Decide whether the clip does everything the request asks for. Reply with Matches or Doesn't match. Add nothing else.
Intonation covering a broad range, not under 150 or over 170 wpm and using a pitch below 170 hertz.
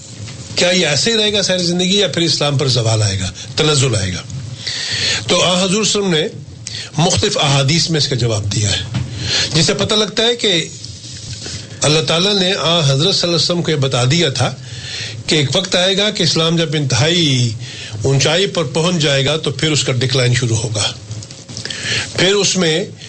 Doesn't match